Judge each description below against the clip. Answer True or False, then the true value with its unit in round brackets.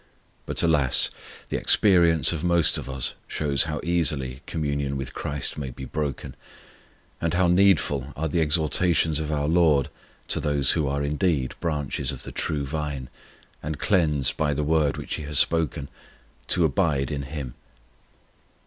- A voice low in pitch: True (75 Hz)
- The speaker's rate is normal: True (160 wpm)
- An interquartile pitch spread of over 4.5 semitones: False (2.6 semitones)